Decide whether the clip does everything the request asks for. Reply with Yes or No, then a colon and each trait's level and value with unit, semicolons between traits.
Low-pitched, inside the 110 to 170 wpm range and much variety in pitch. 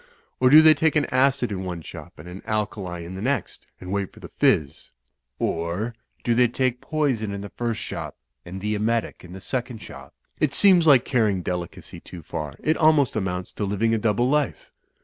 No: low, 110 Hz; fast, 205 wpm; wide, 5.7 semitones